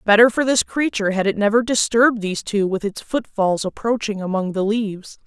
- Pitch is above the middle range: Yes, high, 215 Hz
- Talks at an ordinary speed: Yes, average, 195 wpm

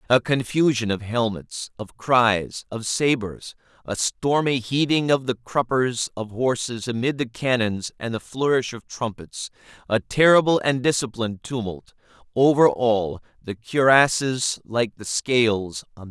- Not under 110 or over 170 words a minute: Yes, average, 145 wpm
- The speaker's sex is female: No, male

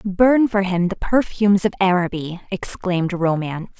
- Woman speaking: Yes, female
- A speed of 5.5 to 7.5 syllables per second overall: No, 4.9 syllables/s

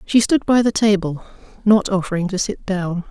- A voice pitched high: Yes, high, 195 Hz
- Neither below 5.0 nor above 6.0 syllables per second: Yes, 5.1 syllables/s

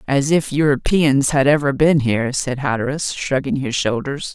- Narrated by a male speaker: No, female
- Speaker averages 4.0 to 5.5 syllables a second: Yes, 4.8 syllables/s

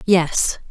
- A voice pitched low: No, medium, 175 Hz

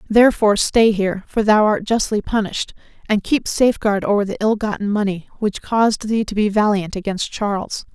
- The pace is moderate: Yes, average, 190 wpm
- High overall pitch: Yes, high, 210 Hz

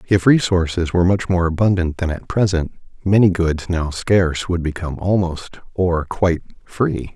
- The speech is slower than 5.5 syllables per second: Yes, 5.0 syllables/s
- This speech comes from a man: Yes, male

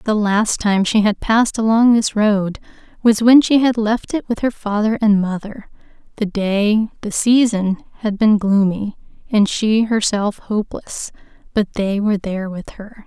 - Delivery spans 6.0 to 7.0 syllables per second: No, 4.4 syllables/s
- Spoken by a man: No, female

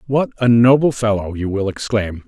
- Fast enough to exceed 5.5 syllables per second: No, 5.0 syllables/s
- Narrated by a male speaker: Yes, male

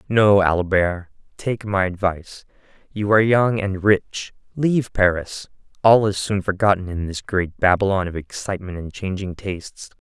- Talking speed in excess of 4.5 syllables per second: Yes, 4.7 syllables/s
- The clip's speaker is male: Yes, male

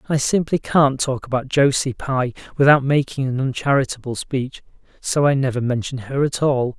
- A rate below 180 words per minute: Yes, average, 170 wpm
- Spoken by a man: Yes, male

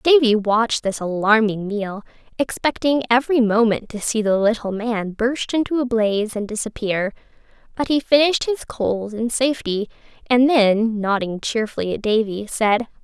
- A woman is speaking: Yes, female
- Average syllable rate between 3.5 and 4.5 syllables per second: No, 4.9 syllables/s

